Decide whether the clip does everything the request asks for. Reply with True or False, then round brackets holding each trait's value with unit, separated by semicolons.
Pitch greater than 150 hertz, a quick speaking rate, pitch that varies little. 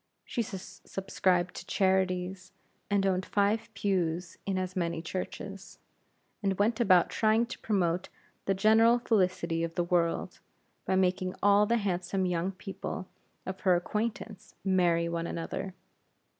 False (190 Hz; 135 wpm; 2.2 semitones)